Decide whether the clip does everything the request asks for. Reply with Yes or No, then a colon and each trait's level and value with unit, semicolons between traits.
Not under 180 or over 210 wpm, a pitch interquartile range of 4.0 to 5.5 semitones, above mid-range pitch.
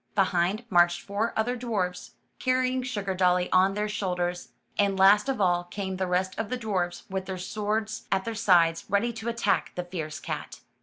No: average, 185 wpm; average, 3.4 semitones; high, 195 Hz